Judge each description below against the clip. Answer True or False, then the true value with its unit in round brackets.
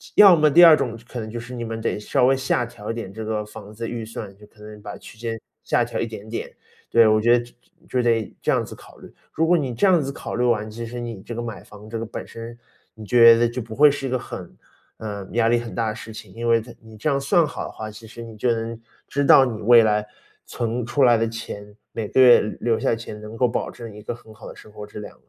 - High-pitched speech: False (115 Hz)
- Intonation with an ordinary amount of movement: False (1.9 semitones)